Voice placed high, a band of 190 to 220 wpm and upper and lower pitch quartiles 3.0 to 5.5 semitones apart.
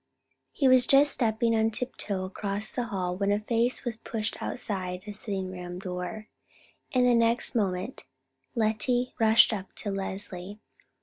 No: high, 215 Hz; average, 150 wpm; average, 3.6 semitones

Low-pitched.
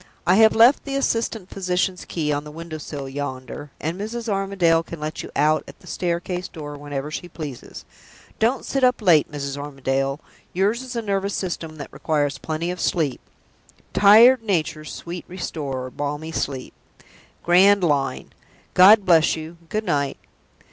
No: medium, 165 Hz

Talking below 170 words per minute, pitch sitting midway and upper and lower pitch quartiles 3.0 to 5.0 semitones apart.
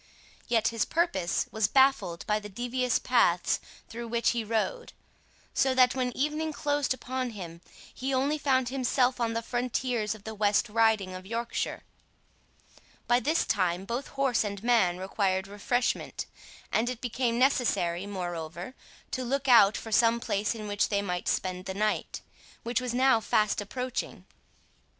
No: average, 155 wpm; high, 230 Hz; average, 3.9 semitones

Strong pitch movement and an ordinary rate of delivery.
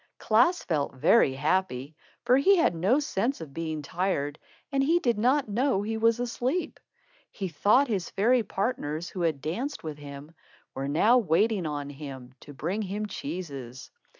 Yes: wide, 8.2 semitones; average, 165 wpm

